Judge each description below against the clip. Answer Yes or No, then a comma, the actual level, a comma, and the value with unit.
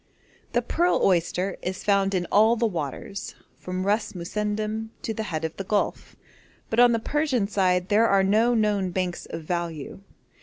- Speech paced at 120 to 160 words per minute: No, average, 175 wpm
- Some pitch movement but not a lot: Yes, average, 3.4 semitones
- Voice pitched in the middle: No, high, 200 Hz